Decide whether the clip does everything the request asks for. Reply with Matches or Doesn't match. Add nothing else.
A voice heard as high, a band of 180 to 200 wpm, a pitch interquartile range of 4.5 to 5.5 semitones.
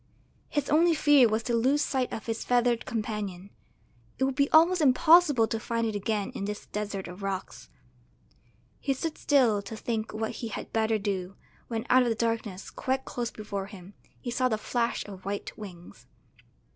Doesn't match